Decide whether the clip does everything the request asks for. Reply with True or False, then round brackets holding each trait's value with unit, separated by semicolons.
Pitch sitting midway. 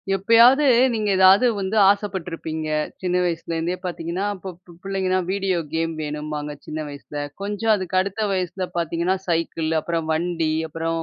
True (180 Hz)